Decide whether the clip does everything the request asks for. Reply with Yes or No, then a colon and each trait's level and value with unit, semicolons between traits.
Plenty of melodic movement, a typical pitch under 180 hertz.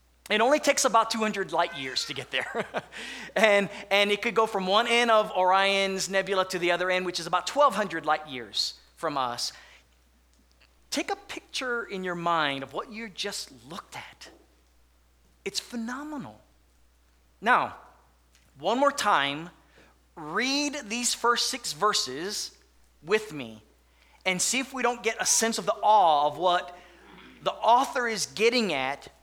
No: wide, 8.6 semitones; high, 190 Hz